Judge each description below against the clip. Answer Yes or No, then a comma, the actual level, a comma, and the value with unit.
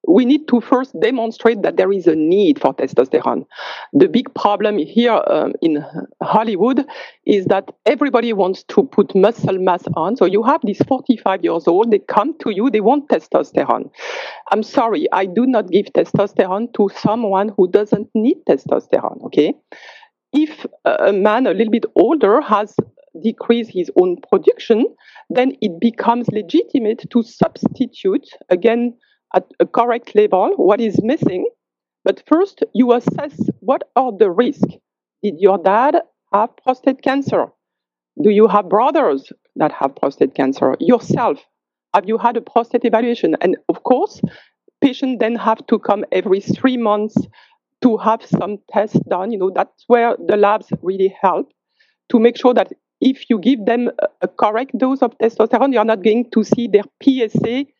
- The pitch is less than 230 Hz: No, high, 235 Hz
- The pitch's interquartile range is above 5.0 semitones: No, average, 4.1 semitones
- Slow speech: No, average, 160 wpm